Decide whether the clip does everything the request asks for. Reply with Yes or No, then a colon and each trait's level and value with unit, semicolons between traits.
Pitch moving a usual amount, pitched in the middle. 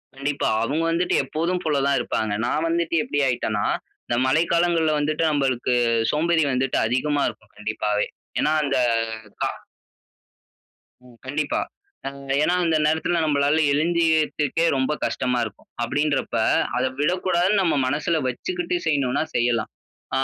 Yes: average, 4.3 semitones; medium, 150 Hz